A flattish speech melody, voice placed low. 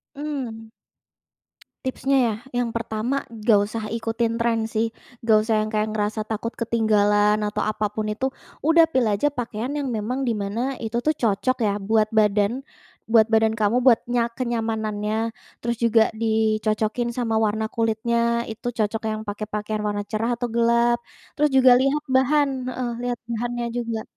No: narrow, 1.9 semitones; high, 225 Hz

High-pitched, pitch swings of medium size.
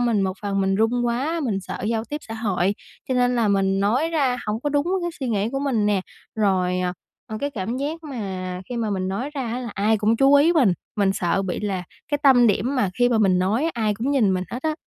Yes: high, 225 Hz; average, 4.9 semitones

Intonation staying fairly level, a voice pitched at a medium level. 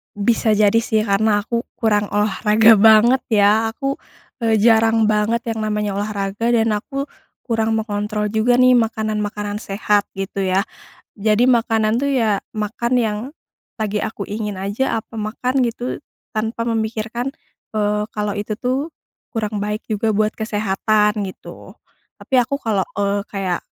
No: narrow, 1.6 semitones; high, 215 Hz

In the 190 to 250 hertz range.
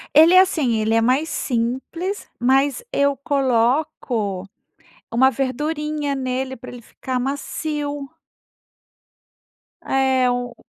No: very high, 265 Hz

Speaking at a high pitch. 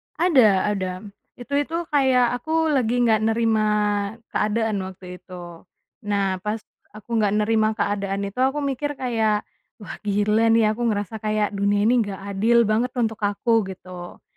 Yes: high, 215 Hz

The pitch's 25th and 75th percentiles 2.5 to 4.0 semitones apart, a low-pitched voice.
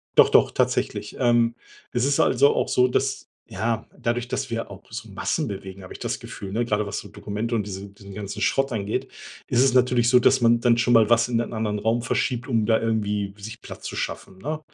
Yes: average, 2.8 semitones; low, 115 Hz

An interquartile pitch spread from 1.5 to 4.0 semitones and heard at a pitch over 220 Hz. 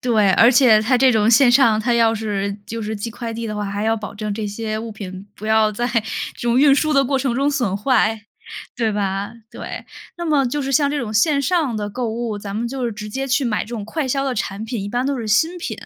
Yes: average, 3.7 semitones; high, 230 Hz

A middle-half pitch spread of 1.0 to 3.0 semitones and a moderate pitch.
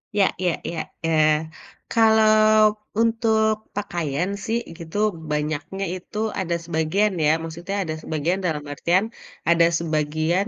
No: average, 5.1 semitones; medium, 175 Hz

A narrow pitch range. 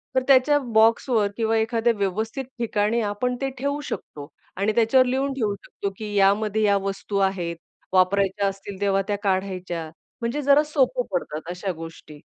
No: average, 3.7 semitones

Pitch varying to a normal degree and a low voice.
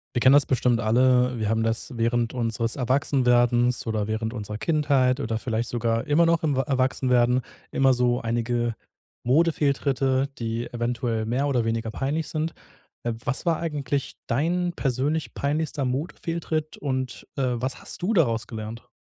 Yes: average, 3.5 semitones; low, 125 Hz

